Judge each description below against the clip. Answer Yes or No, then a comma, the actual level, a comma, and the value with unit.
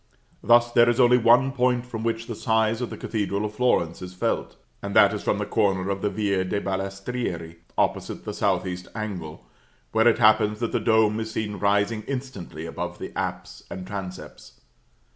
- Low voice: Yes, low, 105 Hz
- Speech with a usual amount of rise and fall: Yes, average, 3.3 semitones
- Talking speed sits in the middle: Yes, average, 190 wpm